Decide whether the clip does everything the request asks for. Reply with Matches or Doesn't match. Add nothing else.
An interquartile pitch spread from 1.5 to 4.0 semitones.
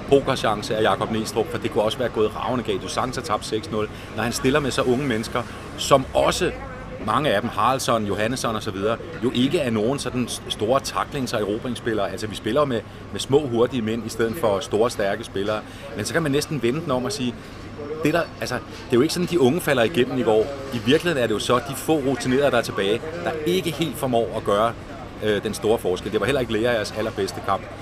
Matches